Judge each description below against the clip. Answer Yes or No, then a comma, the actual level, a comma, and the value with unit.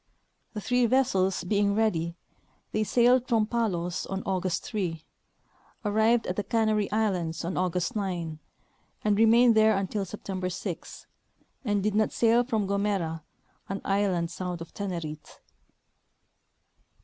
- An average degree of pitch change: Yes, average, 3.4 semitones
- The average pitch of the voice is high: Yes, high, 200 Hz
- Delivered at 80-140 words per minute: Yes, slow, 135 wpm